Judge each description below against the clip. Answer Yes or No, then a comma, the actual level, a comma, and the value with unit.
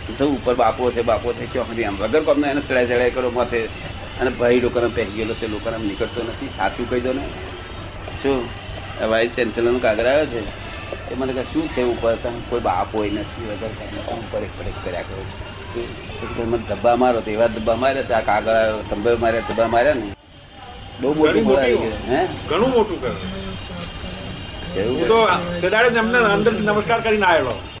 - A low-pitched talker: Yes, low, 115 Hz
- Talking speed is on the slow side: Yes, slow, 45 wpm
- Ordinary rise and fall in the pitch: Yes, average, 3.7 semitones